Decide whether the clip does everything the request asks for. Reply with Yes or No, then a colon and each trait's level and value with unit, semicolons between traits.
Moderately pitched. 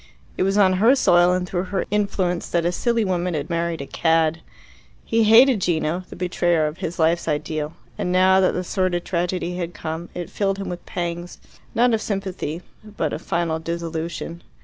Yes: medium, 175 Hz